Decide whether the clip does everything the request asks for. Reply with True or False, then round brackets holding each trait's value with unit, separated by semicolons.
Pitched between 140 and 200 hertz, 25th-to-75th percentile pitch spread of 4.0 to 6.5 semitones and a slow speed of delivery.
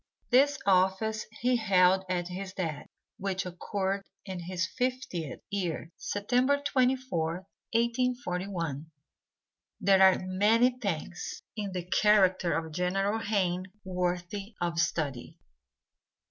False (190 Hz; 3.6 semitones; 105 wpm)